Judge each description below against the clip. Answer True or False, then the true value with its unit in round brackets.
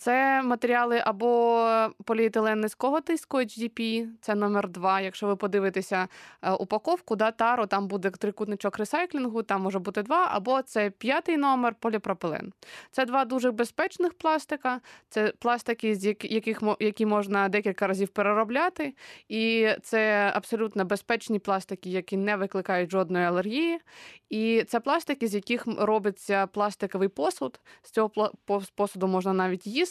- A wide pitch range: False (3.1 semitones)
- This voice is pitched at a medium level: False (220 Hz)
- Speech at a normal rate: True (130 wpm)